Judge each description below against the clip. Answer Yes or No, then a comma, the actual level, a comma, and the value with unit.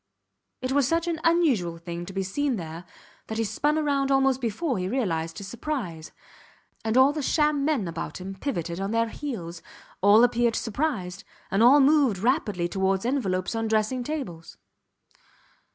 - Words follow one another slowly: No, average, 165 wpm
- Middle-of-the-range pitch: No, high, 225 Hz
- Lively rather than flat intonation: Yes, wide, 7.0 semitones